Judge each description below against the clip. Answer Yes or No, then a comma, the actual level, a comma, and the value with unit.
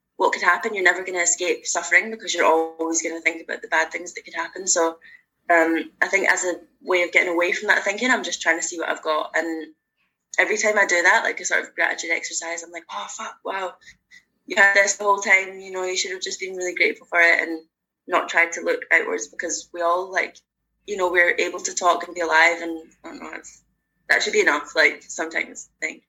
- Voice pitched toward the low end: No, medium, 175 Hz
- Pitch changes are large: No, average, 2.9 semitones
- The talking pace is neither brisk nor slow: No, fast, 250 wpm